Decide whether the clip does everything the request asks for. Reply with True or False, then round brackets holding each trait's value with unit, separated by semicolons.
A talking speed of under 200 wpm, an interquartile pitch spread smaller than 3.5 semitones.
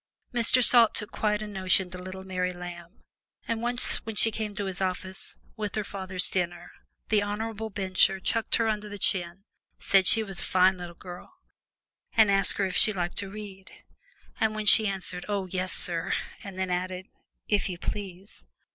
True (185 wpm; 2.5 semitones)